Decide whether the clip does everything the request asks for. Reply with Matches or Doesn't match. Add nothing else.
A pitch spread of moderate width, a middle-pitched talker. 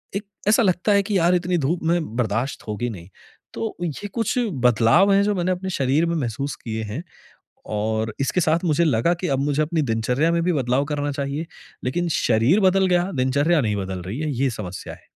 Doesn't match